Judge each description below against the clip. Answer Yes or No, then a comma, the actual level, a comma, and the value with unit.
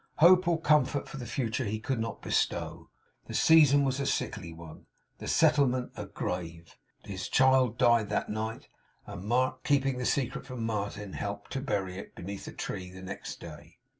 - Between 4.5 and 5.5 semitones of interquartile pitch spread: Yes, average, 5.2 semitones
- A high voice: No, low, 120 Hz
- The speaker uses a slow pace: No, average, 175 wpm